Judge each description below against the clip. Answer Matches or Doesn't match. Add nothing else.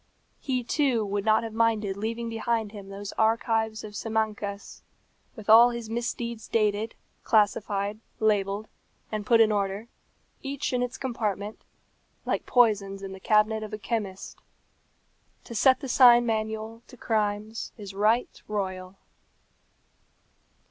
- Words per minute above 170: Doesn't match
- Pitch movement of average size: Doesn't match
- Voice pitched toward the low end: Doesn't match